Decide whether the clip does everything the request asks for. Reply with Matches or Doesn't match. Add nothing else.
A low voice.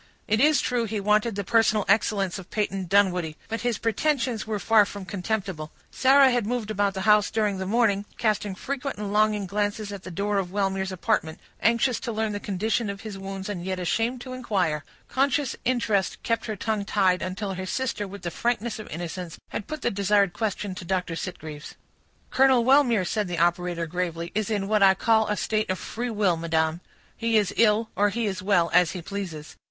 Doesn't match